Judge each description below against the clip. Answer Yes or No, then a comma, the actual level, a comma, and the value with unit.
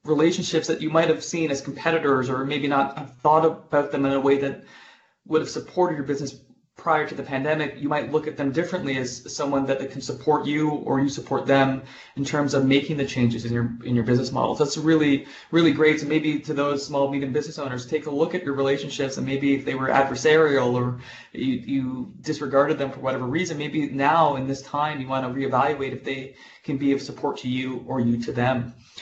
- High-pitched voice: No, medium, 140 Hz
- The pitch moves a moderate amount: No, narrow, 2.3 semitones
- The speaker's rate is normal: No, fast, 225 wpm